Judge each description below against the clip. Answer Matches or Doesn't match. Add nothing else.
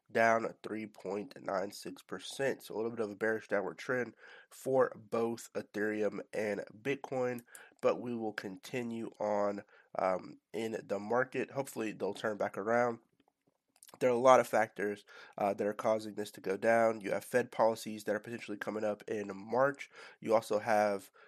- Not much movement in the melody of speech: Matches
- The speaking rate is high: Doesn't match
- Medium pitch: Doesn't match